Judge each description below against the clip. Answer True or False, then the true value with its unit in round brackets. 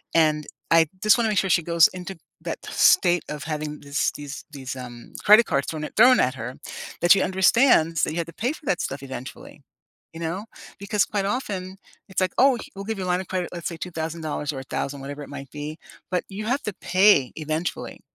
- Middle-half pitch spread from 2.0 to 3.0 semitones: False (4.7 semitones)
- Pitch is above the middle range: False (170 Hz)